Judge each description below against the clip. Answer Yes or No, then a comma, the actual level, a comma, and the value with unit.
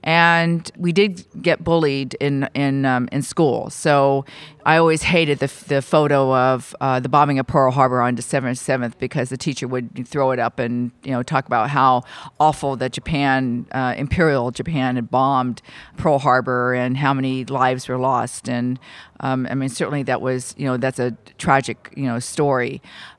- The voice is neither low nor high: No, low, 130 Hz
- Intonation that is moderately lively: No, narrow, 2.3 semitones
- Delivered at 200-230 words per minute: No, average, 185 wpm